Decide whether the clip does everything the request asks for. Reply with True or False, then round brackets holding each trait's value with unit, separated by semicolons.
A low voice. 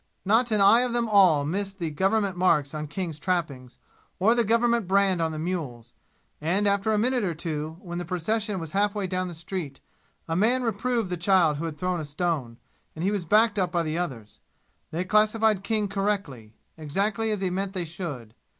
False (185 Hz)